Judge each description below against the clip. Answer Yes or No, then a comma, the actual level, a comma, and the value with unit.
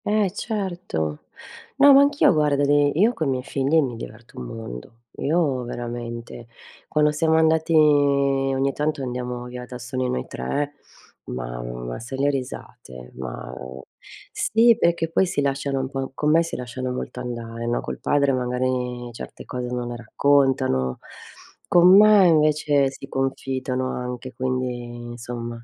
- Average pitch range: Yes, average, 3.8 semitones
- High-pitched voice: No, low, 130 Hz